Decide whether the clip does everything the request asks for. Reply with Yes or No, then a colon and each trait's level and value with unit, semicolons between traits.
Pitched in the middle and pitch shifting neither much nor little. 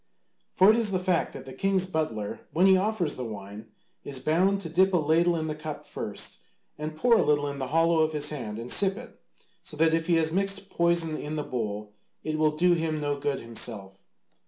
Yes: medium, 155 Hz; average, 4.3 semitones